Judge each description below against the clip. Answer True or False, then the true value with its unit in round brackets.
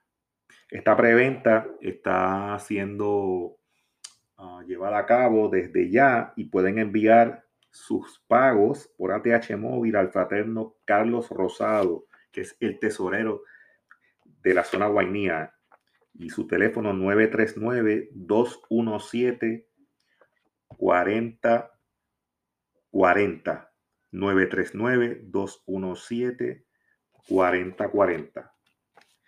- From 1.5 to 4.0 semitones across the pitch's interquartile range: True (2.9 semitones)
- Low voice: True (110 Hz)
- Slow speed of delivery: True (70 wpm)